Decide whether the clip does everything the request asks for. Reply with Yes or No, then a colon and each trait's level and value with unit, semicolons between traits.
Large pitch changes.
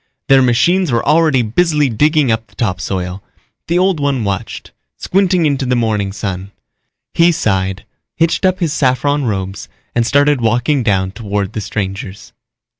Yes: wide, 7.1 semitones